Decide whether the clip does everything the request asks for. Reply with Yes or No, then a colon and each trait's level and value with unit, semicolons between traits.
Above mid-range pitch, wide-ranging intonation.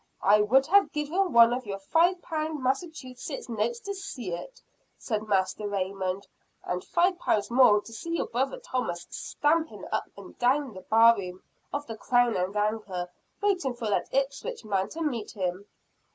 Yes: high, 235 Hz; wide, 7.0 semitones